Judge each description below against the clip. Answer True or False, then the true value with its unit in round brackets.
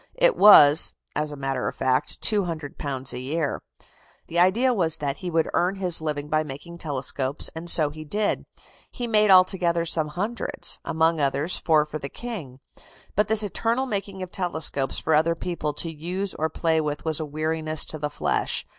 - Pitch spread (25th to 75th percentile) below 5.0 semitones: True (3.8 semitones)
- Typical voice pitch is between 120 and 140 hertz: False (160 Hz)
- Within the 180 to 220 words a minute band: True (185 wpm)